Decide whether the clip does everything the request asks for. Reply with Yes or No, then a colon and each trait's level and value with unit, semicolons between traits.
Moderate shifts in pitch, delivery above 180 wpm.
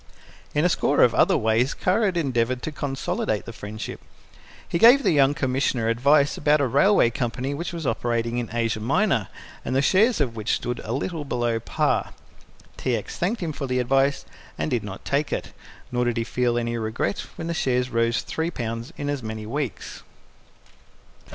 Yes: average, 4.2 semitones; average, 190 wpm